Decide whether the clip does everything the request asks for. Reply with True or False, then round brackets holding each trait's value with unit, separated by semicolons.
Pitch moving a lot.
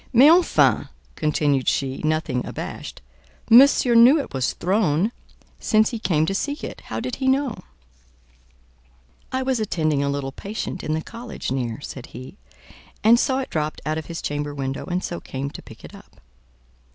True (8.5 semitones)